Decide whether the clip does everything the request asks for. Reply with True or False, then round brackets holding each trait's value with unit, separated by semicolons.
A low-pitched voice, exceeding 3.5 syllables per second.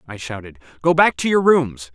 True (130 Hz; 5.2 syllables/s)